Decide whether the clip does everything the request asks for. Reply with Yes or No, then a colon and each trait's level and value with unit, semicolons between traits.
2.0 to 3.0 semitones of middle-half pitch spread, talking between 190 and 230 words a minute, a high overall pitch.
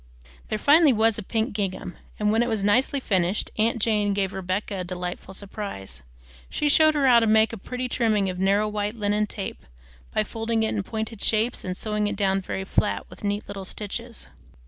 Yes: narrow, 2.5 semitones; average, 200 wpm; high, 210 Hz